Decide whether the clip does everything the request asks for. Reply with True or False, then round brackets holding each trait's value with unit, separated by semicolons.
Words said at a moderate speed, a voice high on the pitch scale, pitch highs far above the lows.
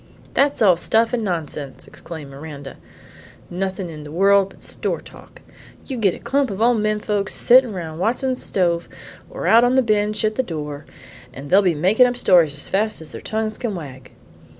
True (185 wpm; 195 Hz; 5.7 semitones)